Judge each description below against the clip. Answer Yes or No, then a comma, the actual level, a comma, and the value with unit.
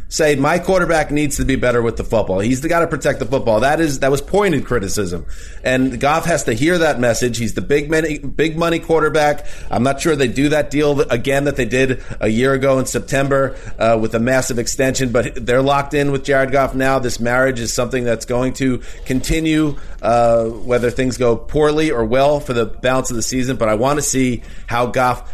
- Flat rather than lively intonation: No, average, 3.3 semitones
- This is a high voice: No, low, 130 Hz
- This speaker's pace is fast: Yes, fast, 220 wpm